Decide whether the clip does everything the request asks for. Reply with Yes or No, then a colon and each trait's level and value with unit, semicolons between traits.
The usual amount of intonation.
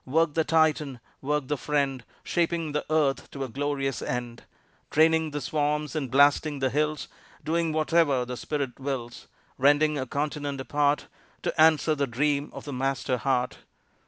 No: narrow, 2.3 semitones